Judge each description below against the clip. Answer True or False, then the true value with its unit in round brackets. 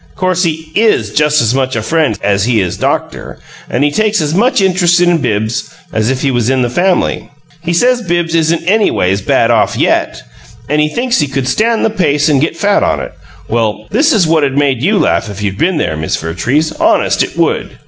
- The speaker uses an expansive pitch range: True (6.8 semitones)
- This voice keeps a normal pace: False (220 wpm)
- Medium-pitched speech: True (150 Hz)